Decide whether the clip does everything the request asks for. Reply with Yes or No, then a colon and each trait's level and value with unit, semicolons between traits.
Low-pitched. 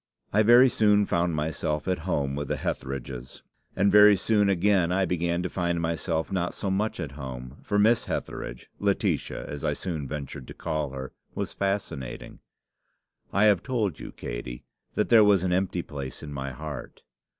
Yes: very low, 85 Hz